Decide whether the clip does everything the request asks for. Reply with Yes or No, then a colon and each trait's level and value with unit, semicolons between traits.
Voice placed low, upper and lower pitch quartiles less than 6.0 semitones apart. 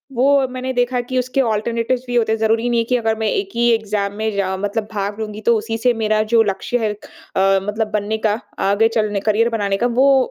No: high, 225 Hz; narrow, 2.6 semitones